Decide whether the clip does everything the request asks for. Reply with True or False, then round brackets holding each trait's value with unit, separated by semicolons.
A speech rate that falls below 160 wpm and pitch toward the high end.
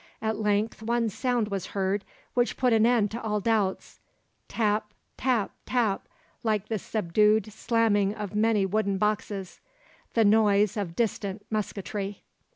True (140 wpm; 210 Hz)